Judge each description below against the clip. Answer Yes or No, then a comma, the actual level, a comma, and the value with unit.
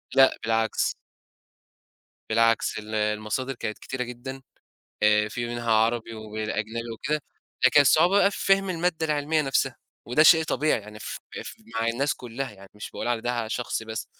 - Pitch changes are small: No, average, 4.2 semitones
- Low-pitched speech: Yes, low, 120 Hz